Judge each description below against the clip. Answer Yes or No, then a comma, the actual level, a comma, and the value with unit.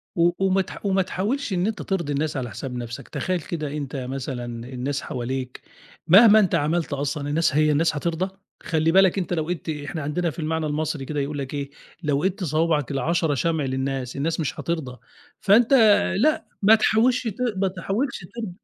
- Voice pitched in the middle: Yes, medium, 155 Hz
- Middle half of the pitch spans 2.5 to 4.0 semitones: No, average, 5.0 semitones